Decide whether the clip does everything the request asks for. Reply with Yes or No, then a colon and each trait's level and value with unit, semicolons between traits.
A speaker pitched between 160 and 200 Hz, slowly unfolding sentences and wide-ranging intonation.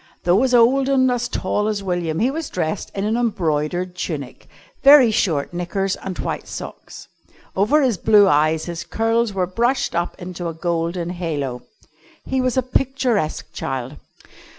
No: high, 190 Hz; average, 160 wpm; wide, 6.1 semitones